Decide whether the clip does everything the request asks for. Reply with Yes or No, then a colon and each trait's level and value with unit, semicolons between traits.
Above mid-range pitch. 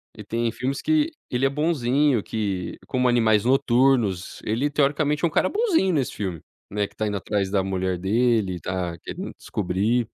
No: low, 115 Hz